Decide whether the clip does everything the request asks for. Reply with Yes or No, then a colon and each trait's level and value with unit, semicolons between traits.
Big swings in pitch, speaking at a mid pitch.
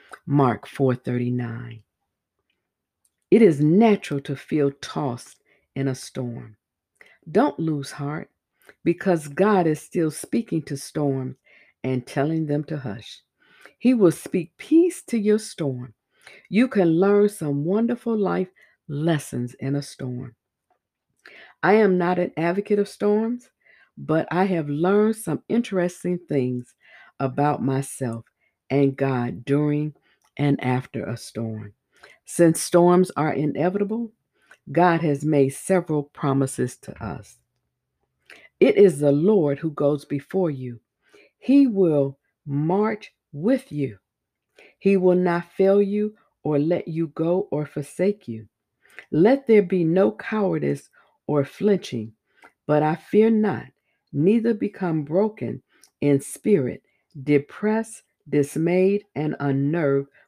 Yes: wide, 5.8 semitones; medium, 155 Hz